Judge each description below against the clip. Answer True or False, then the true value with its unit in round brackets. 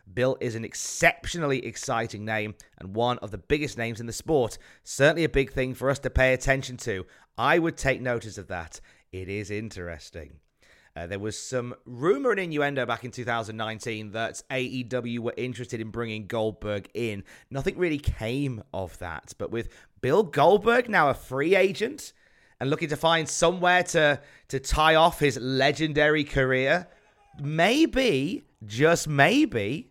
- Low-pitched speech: True (125 Hz)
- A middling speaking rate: True (160 wpm)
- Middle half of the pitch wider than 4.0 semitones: True (5.2 semitones)